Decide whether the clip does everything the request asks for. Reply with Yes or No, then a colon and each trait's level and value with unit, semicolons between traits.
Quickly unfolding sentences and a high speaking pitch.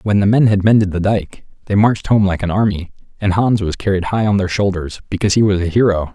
No: fast, 255 wpm; low, 100 Hz